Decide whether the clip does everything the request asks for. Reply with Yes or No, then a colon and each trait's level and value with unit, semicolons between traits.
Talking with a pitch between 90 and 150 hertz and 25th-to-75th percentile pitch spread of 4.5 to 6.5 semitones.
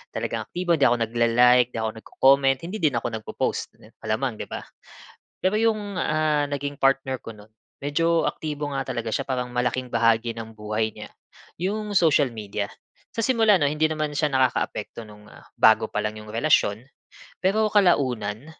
Yes: low, 135 Hz; wide, 5.5 semitones